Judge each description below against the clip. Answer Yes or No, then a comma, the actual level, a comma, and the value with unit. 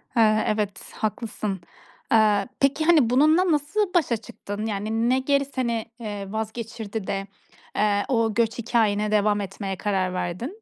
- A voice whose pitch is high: Yes, high, 220 Hz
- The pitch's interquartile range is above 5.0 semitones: No, average, 3.5 semitones